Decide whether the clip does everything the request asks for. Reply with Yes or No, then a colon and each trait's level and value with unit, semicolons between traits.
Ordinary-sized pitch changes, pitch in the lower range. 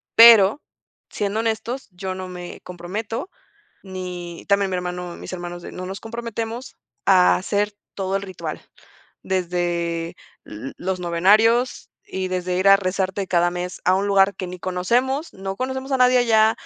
No: average, 3.5 semitones; high, 190 Hz